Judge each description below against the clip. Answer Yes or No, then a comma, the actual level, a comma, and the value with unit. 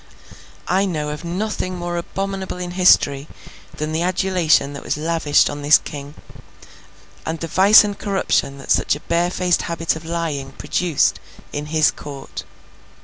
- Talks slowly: No, average, 150 wpm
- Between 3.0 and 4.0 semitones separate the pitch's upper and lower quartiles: Yes, average, 3.4 semitones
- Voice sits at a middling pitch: Yes, medium, 170 Hz